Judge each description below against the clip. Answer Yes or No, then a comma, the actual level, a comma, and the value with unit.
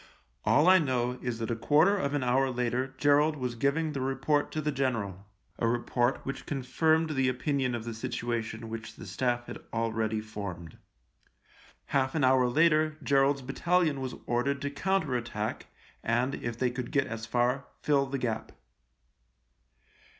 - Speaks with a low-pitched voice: Yes, low, 130 Hz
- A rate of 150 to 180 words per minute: Yes, average, 165 wpm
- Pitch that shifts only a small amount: No, average, 3.4 semitones